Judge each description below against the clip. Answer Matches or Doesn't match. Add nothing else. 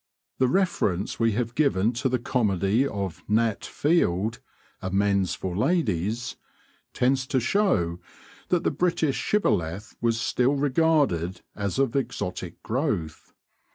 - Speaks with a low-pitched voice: Matches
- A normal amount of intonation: Doesn't match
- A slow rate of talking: Matches